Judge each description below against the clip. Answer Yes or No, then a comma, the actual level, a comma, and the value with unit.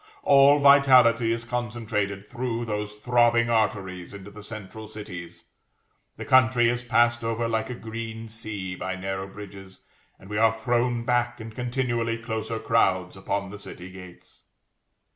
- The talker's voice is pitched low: Yes, low, 115 Hz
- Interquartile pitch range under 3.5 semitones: Yes, average, 2.9 semitones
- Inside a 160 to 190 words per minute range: No, average, 145 wpm